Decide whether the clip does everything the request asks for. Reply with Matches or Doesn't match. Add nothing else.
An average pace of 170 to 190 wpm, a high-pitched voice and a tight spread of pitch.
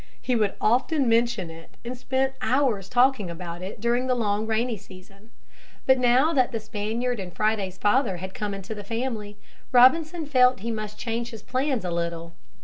Doesn't match